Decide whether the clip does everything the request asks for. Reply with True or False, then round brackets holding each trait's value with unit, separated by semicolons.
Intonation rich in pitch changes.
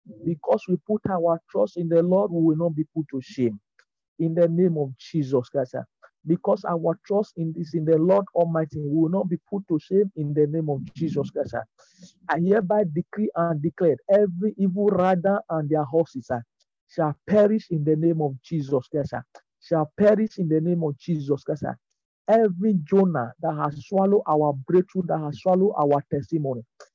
False (3.9 semitones)